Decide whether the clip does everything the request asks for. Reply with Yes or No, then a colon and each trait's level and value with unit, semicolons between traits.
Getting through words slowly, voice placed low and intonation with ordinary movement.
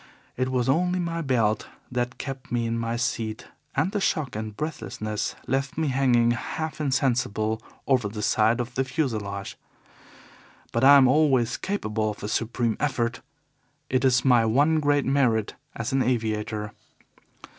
No: average, 155 wpm; low, 125 Hz; average, 3.6 semitones